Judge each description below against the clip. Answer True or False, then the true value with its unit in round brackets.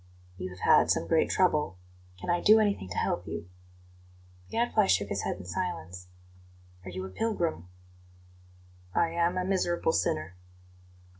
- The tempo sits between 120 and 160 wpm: True (155 wpm)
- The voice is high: False (160 Hz)